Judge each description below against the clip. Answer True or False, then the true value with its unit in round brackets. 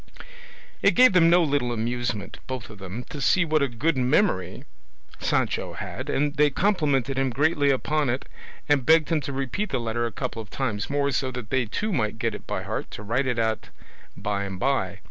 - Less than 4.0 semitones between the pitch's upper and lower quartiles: False (4.4 semitones)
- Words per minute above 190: True (205 wpm)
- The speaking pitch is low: True (130 Hz)